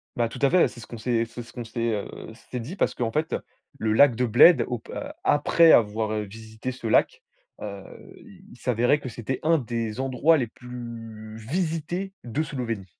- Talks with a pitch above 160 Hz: No, low, 120 Hz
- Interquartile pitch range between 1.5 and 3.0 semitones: No, average, 4.2 semitones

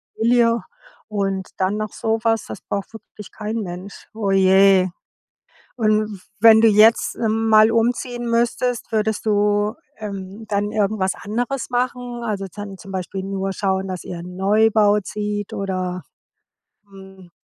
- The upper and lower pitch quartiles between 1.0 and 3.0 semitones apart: Yes, narrow, 2.5 semitones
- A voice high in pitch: Yes, high, 210 Hz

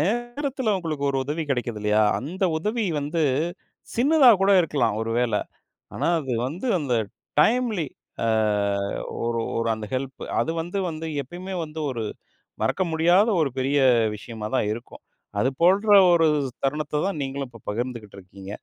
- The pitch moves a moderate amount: No, wide, 7.7 semitones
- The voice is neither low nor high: Yes, medium, 150 Hz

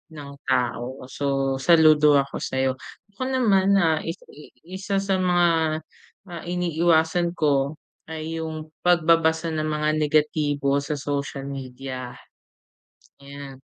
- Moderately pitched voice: Yes, medium, 155 Hz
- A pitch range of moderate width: Yes, average, 3.4 semitones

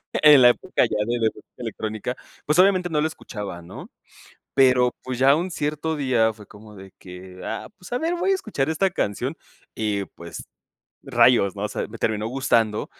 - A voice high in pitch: No, low, 125 Hz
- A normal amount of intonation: No, wide, 6.2 semitones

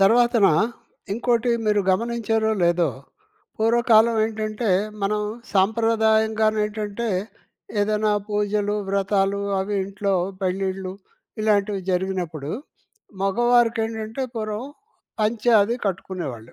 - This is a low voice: No, high, 210 Hz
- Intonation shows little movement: Yes, narrow, 2.3 semitones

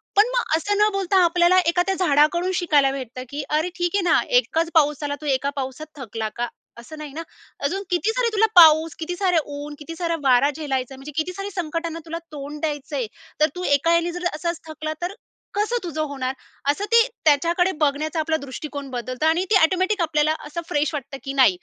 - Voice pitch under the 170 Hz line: No, very high, 315 Hz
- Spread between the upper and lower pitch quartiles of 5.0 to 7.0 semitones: No, average, 3.7 semitones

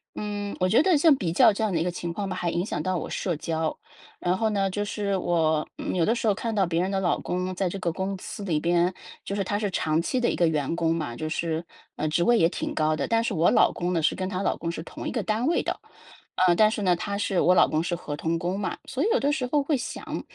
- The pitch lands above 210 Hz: No, medium, 185 Hz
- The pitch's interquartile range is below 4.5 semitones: Yes, average, 3.6 semitones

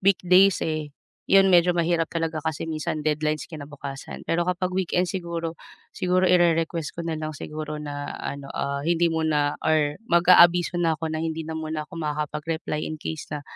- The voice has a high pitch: No, medium, 160 Hz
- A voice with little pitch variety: Yes, narrow, 2.2 semitones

